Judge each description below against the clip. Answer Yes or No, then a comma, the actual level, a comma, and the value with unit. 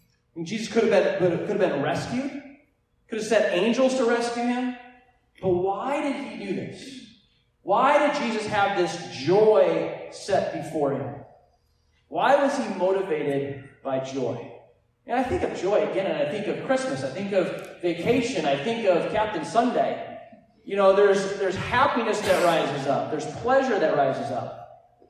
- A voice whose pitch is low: No, high, 210 Hz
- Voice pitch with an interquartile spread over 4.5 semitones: Yes, average, 5.2 semitones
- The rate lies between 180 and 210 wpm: No, average, 165 wpm